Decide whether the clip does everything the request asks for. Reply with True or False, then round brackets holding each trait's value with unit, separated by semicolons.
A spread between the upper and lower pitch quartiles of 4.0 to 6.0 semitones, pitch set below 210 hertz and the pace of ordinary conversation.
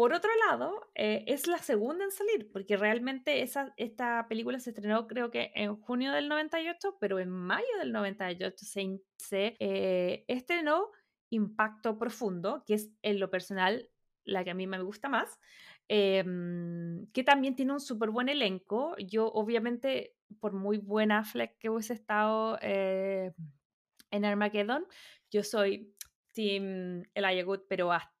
False (4.4 semitones; 215 Hz; 155 wpm)